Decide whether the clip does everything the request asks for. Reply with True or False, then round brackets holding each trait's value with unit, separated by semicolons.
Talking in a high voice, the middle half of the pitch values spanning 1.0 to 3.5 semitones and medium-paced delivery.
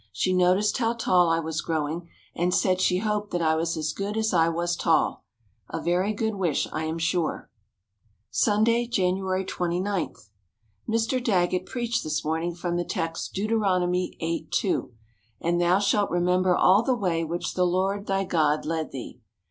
False (180 Hz; 3.2 semitones; 170 wpm)